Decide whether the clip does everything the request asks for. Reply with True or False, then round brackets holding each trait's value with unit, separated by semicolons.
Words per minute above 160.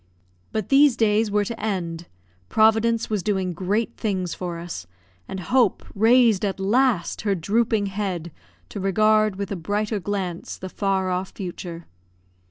False (150 wpm)